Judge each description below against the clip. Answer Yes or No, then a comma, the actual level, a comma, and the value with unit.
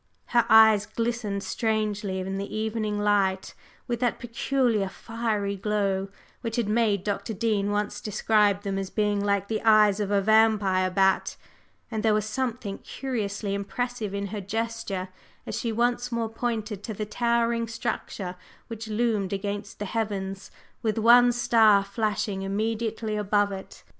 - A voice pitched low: No, high, 210 Hz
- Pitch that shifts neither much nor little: No, narrow, 2.3 semitones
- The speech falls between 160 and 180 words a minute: No, average, 150 wpm